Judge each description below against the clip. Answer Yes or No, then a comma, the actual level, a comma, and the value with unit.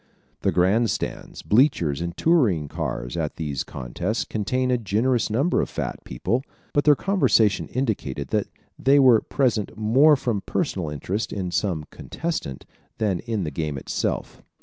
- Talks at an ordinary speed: Yes, average, 150 wpm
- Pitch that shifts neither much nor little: No, wide, 7.9 semitones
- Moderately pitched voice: No, low, 105 Hz